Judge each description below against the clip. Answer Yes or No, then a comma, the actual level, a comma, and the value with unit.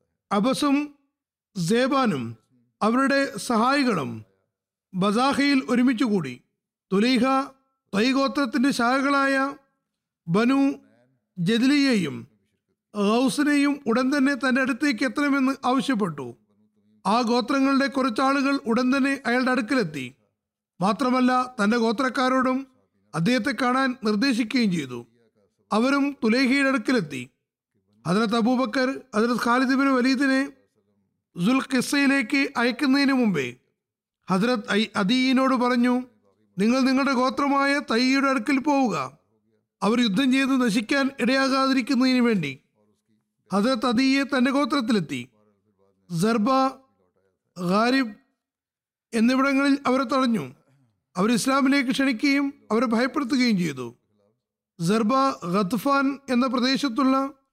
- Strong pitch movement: Yes, wide, 5.8 semitones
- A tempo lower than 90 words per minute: Yes, average, 80 wpm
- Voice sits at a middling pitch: No, very high, 250 Hz